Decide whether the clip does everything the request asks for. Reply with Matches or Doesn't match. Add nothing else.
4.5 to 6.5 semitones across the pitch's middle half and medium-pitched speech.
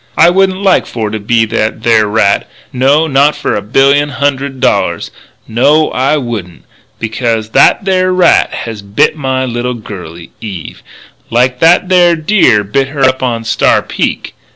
Doesn't match